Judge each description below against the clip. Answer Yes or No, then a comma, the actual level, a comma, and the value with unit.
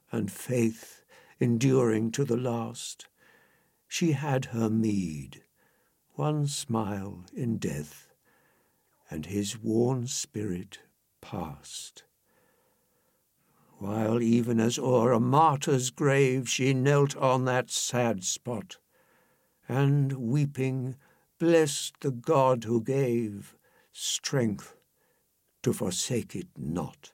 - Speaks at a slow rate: Yes, slow, 95 wpm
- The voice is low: Yes, low, 125 Hz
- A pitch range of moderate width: Yes, average, 3.6 semitones